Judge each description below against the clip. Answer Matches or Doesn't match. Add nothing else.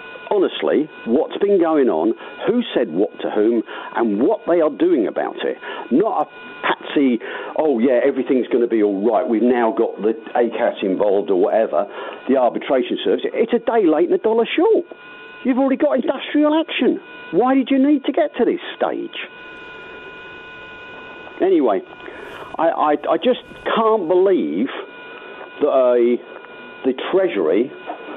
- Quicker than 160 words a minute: Doesn't match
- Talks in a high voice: Matches